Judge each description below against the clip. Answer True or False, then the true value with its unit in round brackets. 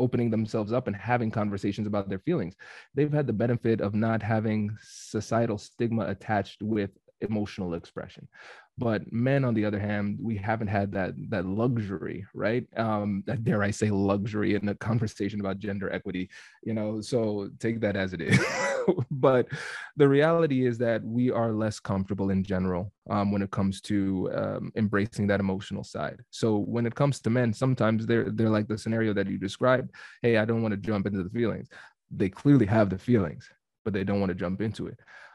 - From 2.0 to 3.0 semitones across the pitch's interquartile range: True (2.5 semitones)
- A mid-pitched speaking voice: False (110 Hz)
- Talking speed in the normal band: True (190 wpm)